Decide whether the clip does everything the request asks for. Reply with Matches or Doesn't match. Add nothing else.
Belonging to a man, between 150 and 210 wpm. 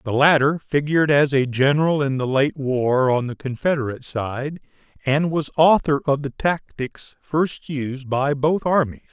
Matches